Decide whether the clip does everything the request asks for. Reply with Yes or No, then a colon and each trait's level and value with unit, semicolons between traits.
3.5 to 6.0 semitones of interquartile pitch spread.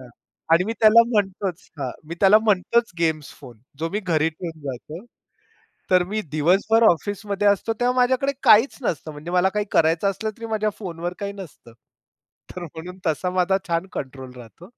Yes: average, 4.6 semitones